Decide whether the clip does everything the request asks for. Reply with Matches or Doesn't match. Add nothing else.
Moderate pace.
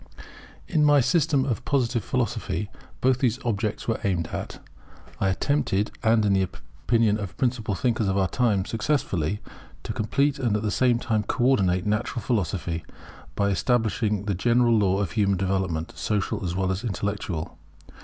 Matches